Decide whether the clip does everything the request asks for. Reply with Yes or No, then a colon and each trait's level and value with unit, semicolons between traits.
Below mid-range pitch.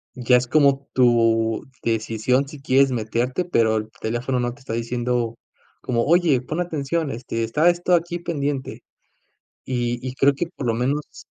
Yes: low, 125 Hz